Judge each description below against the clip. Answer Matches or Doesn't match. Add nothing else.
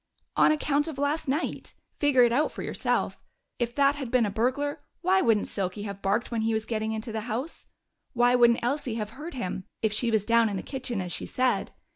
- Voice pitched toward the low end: Doesn't match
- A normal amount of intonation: Matches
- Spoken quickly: Matches